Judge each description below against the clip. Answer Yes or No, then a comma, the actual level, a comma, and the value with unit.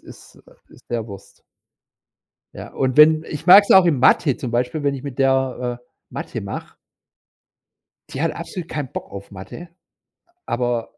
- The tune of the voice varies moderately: Yes, average, 4.2 semitones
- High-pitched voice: No, low, 135 Hz